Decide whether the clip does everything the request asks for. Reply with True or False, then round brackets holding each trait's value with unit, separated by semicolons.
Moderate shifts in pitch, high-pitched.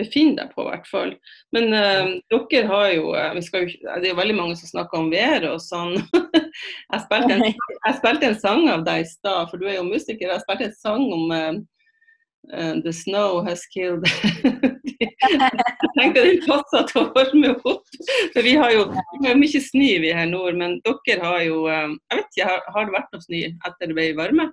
False (7.8 semitones; 215 Hz)